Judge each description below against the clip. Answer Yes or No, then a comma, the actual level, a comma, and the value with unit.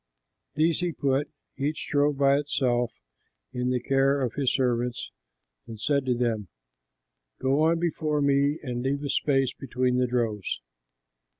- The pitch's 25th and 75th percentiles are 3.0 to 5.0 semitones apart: No, narrow, 2.5 semitones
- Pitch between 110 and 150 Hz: Yes, low, 135 Hz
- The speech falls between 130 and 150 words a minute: Yes, average, 145 wpm